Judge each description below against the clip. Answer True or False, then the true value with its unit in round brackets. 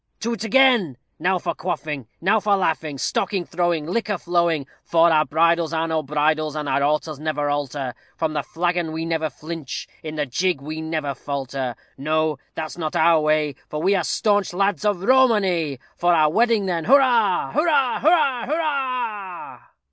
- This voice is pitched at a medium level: True (165 Hz)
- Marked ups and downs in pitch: False (4.8 semitones)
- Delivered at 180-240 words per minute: False (170 wpm)